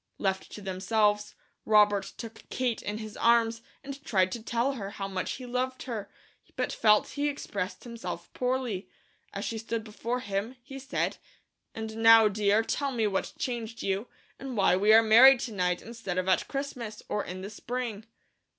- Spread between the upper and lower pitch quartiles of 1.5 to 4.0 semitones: Yes, average, 3.3 semitones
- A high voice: Yes, high, 220 Hz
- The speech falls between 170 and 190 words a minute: Yes, average, 180 wpm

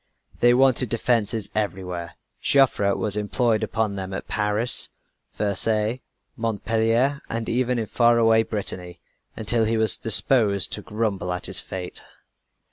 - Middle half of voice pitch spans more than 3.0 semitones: No, narrow, 2.6 semitones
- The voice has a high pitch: No, low, 110 Hz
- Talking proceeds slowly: Yes, slow, 125 wpm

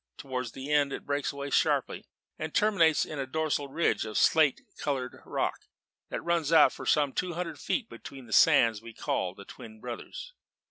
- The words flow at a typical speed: Yes, average, 185 wpm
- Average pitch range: Yes, average, 4.0 semitones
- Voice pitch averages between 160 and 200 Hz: No, medium, 140 Hz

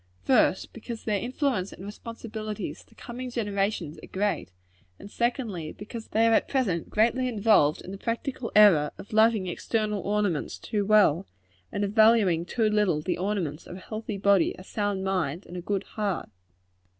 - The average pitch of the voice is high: Yes, high, 205 Hz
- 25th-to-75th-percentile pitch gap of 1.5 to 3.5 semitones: Yes, average, 3.1 semitones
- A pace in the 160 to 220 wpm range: Yes, average, 170 wpm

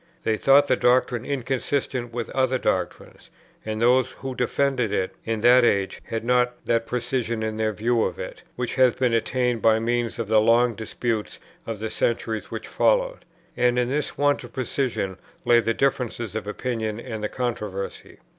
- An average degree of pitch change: No, narrow, 2.3 semitones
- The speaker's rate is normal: Yes, average, 175 wpm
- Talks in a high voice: No, low, 120 Hz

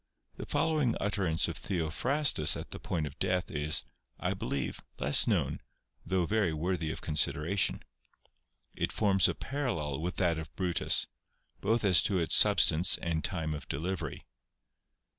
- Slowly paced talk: No, average, 150 wpm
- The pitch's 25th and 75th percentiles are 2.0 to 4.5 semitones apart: Yes, average, 4.2 semitones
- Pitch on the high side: No, very low, 85 Hz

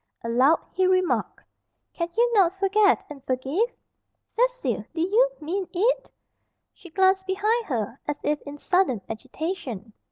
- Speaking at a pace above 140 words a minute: No, slow, 135 wpm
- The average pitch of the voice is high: Yes, very high, 365 Hz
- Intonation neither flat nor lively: No, wide, 5.9 semitones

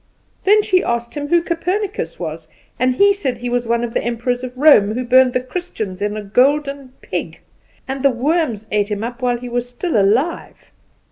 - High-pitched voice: Yes, very high, 250 Hz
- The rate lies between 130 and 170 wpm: No, average, 200 wpm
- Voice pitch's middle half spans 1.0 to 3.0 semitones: No, average, 3.9 semitones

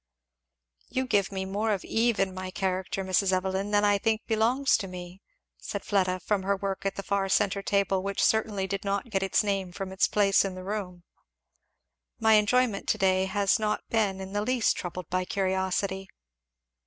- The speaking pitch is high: Yes, high, 195 Hz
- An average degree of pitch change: No, narrow, 1.6 semitones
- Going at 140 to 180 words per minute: No, average, 190 wpm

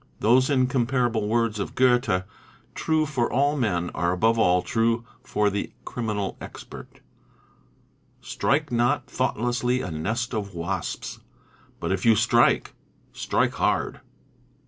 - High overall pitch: No, low, 115 Hz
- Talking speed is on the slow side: Yes, slow, 125 wpm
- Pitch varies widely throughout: No, average, 4.1 semitones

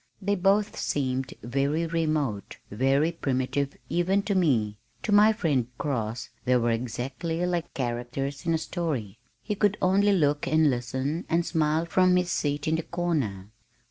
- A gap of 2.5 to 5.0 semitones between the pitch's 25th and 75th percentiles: No, wide, 5.4 semitones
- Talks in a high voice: No, medium, 150 Hz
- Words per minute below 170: Yes, average, 155 wpm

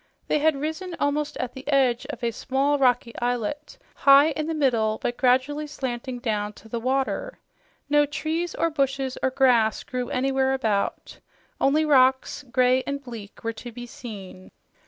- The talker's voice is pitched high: Yes, very high, 265 Hz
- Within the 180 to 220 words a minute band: No, average, 165 wpm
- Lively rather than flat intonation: No, average, 3.3 semitones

